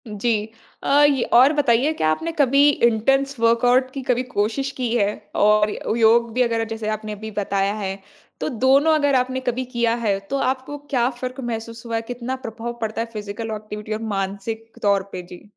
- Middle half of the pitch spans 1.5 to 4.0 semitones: Yes, average, 3.4 semitones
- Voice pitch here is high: Yes, high, 230 Hz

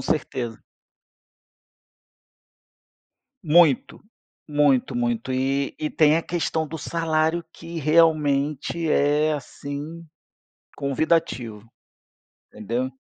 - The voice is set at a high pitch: No, medium, 150 Hz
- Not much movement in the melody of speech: No, average, 3.4 semitones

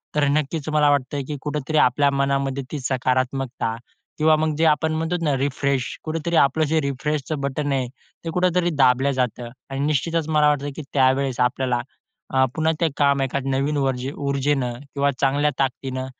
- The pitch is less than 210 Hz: Yes, medium, 140 Hz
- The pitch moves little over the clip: Yes, narrow, 2.3 semitones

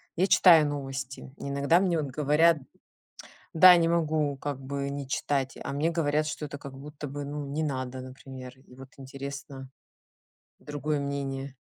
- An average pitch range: No, narrow, 2.1 semitones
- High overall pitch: No, medium, 140 Hz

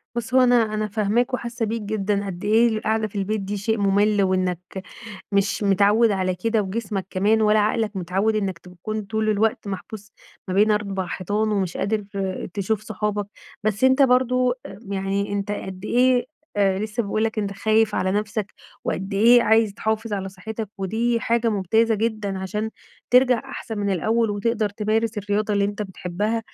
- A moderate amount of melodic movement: No, narrow, 2.0 semitones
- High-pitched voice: Yes, high, 210 Hz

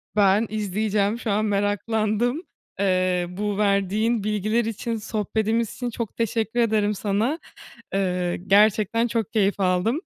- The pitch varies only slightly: Yes, narrow, 2.3 semitones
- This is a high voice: Yes, high, 210 Hz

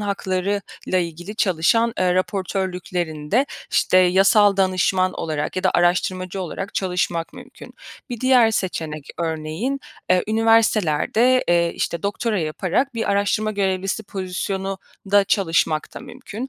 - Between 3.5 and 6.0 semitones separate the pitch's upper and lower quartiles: No, average, 3.1 semitones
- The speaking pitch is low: No, high, 190 Hz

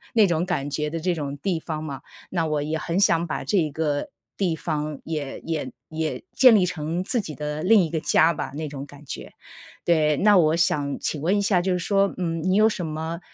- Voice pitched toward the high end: No, medium, 160 Hz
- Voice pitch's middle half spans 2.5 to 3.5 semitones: Yes, average, 3.1 semitones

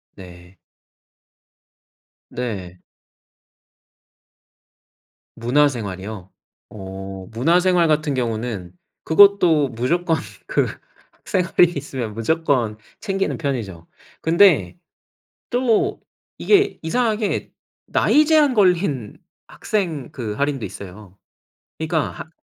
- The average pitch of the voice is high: No, medium, 140 Hz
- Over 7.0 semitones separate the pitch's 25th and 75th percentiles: Yes, wide, 8.8 semitones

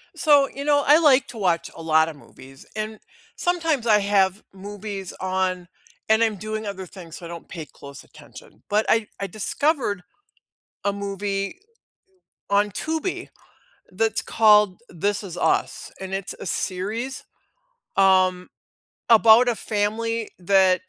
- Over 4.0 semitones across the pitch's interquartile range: No, average, 3.3 semitones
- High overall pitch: Yes, high, 205 Hz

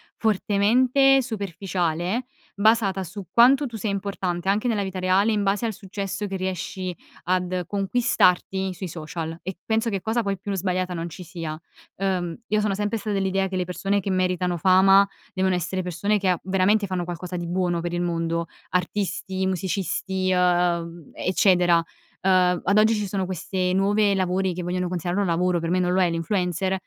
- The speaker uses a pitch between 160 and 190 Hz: Yes, medium, 185 Hz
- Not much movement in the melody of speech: Yes, narrow, 2.1 semitones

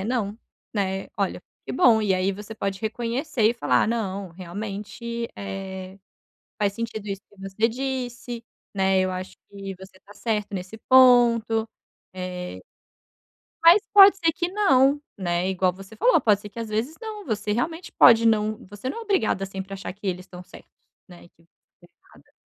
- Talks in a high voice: Yes, high, 210 Hz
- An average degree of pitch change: Yes, average, 3.8 semitones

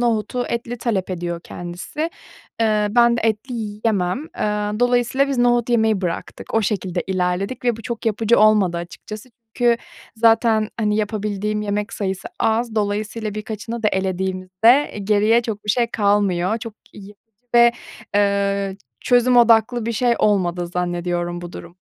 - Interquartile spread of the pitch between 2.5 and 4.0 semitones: Yes, average, 3.2 semitones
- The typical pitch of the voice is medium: No, high, 210 Hz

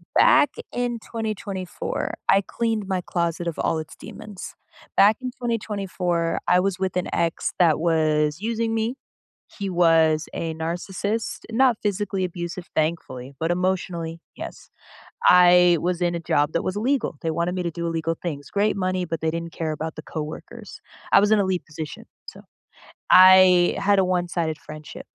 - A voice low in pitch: No, medium, 180 Hz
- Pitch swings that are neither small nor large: Yes, average, 3.3 semitones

